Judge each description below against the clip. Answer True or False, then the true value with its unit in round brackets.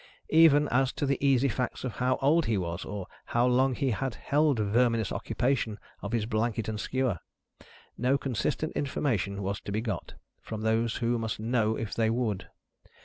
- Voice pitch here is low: True (120 Hz)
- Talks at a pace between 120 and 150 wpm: False (180 wpm)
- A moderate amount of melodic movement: True (3.6 semitones)